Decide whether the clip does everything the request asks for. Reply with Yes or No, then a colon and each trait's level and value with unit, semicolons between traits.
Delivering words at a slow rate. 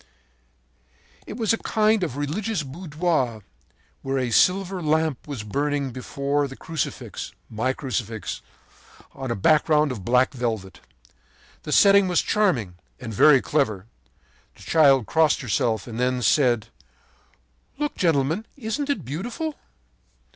Yes: slow, 125 wpm